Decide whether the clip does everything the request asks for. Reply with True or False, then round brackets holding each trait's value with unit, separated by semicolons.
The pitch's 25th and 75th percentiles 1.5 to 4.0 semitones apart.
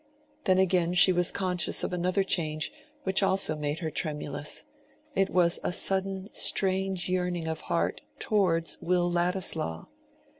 True (2.6 semitones)